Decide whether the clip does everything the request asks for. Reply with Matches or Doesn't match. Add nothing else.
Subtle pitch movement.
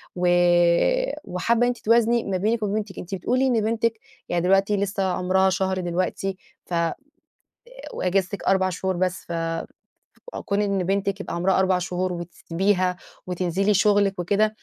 Matches